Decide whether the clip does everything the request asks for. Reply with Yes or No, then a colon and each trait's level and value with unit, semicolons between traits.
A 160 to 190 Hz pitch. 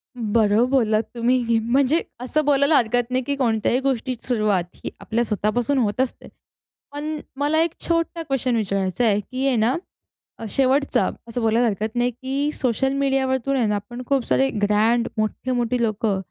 No: high, 245 Hz